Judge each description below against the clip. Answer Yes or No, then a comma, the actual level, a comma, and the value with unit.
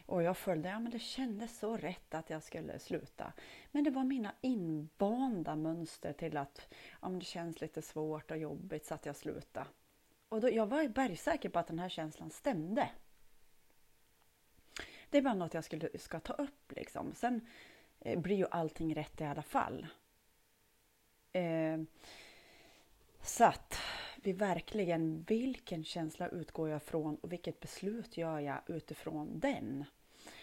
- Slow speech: No, average, 160 wpm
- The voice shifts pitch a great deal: Yes, wide, 5.9 semitones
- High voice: No, medium, 170 Hz